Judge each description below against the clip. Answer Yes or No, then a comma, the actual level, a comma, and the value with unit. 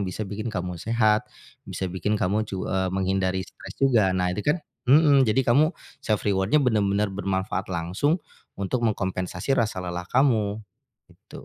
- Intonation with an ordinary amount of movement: Yes, average, 3.4 semitones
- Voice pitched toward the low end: Yes, low, 100 Hz